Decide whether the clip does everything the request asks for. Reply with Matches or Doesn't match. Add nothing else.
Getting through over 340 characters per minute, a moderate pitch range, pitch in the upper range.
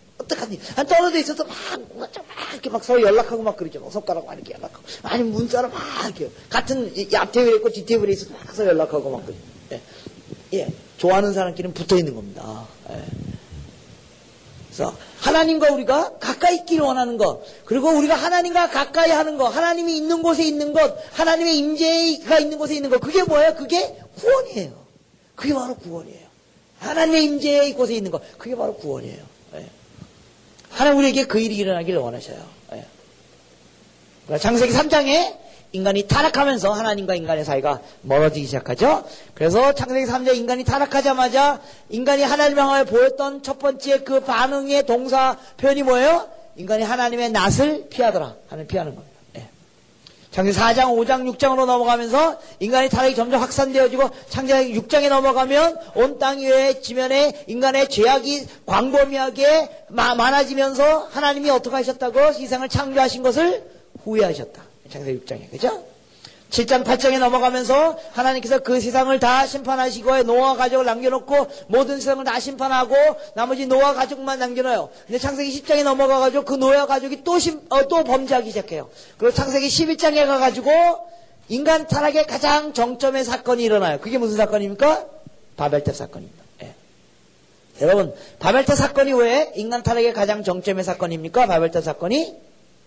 Matches